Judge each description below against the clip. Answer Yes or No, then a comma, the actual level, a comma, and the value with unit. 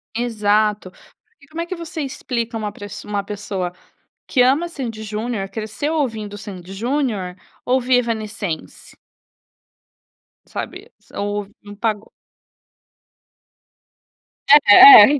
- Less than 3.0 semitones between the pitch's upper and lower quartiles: No, average, 3.7 semitones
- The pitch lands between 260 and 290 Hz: No, high, 220 Hz